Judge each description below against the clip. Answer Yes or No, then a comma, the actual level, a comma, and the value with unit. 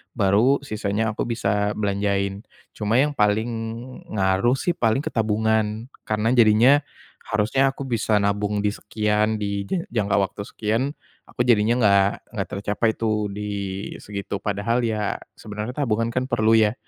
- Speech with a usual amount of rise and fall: No, narrow, 2.2 semitones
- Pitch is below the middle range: Yes, low, 110 Hz